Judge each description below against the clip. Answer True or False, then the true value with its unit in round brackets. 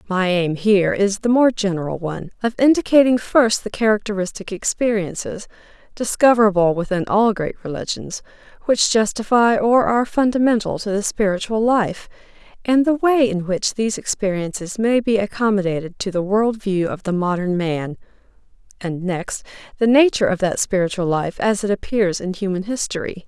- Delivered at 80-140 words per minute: False (150 wpm)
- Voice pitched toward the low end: False (205 Hz)